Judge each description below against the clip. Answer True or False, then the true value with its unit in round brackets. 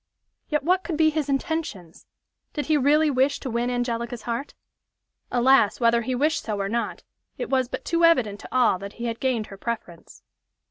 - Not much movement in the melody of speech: False (4.3 semitones)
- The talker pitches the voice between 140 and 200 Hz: False (250 Hz)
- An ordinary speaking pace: True (190 wpm)